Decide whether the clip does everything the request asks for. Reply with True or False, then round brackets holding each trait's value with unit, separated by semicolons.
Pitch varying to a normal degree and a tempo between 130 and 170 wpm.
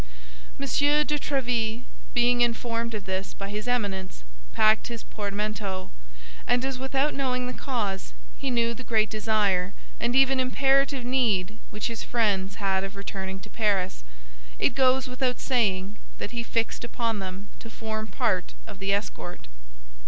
True (4.1 semitones; 150 wpm)